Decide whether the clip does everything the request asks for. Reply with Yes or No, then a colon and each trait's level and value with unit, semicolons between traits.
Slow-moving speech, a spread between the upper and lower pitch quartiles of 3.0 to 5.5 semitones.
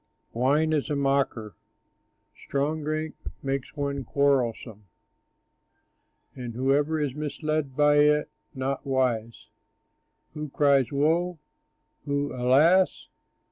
No: slow, 100 wpm; narrow, 2.5 semitones